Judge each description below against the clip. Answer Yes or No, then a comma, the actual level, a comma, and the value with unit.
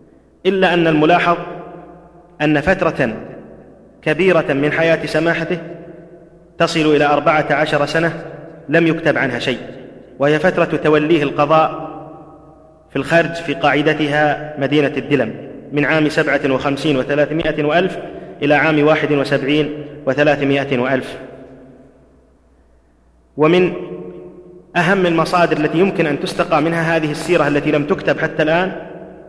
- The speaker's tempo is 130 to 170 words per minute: No, average, 115 wpm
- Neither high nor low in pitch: Yes, medium, 155 Hz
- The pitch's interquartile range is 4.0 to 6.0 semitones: No, narrow, 2.6 semitones